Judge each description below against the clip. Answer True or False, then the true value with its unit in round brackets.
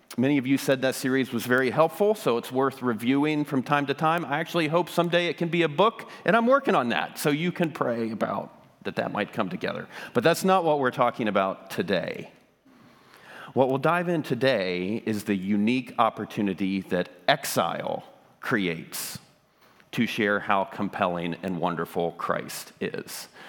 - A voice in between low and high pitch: False (130 Hz)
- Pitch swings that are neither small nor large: False (7.6 semitones)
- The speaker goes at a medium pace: True (175 wpm)